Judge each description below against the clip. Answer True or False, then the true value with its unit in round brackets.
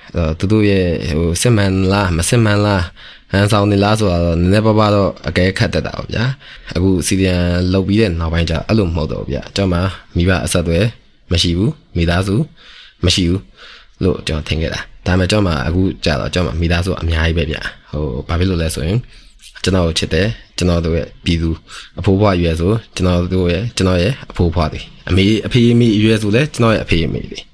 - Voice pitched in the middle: False (90 Hz)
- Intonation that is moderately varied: True (3.5 semitones)